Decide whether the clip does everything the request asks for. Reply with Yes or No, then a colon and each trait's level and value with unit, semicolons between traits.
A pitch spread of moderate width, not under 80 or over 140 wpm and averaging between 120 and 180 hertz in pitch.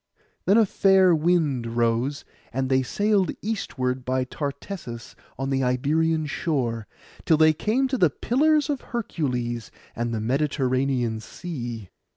No: wide, 6.3 semitones; slow, 135 wpm; medium, 140 Hz